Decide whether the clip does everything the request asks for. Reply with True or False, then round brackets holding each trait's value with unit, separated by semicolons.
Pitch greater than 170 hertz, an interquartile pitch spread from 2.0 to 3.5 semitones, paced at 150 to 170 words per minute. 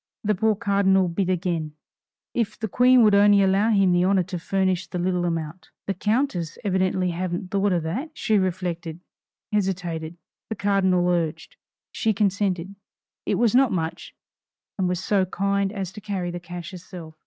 True (185 Hz; 2.4 semitones; 165 wpm)